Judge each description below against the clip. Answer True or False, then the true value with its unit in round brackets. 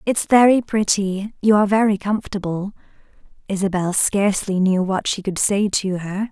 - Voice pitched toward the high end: True (200 Hz)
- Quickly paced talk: False (145 wpm)